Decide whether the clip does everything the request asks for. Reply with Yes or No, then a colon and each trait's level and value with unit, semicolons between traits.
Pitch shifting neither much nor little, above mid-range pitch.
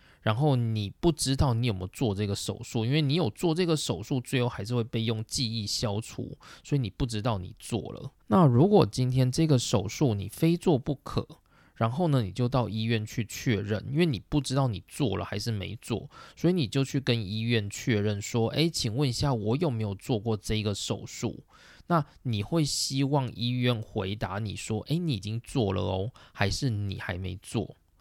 No: average, 4.4 semitones; low, 120 Hz